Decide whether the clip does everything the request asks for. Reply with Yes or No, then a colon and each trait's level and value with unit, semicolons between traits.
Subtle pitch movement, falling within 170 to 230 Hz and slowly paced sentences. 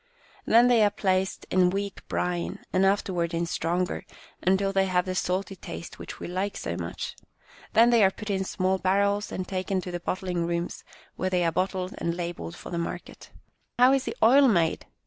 No: narrow, 2.2 semitones; medium, 185 Hz; fast, 205 wpm